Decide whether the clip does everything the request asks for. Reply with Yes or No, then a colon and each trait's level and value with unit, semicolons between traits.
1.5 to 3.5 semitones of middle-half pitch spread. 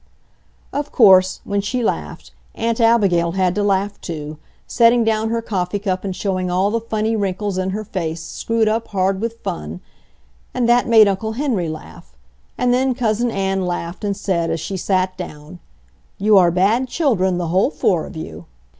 No: average, 3.9 semitones